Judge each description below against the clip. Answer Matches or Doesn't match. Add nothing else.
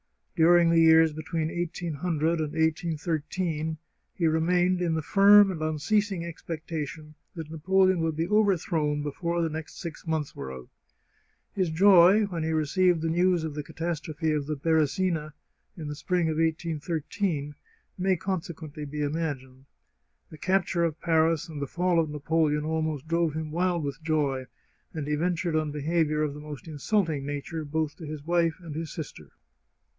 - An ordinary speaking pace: Matches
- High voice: Doesn't match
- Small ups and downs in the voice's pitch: Matches